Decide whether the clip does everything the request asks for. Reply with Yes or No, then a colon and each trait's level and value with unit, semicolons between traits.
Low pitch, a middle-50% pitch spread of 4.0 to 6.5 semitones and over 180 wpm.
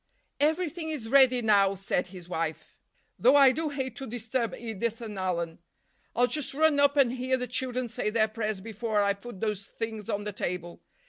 No: high, 230 Hz; average, 4.4 semitones; average, 190 wpm